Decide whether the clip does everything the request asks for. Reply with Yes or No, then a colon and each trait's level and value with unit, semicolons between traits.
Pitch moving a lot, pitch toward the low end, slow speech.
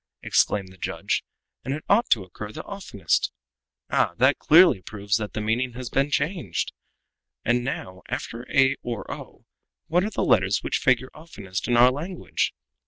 No: wide, 6.0 semitones; low, 120 Hz; average, 170 wpm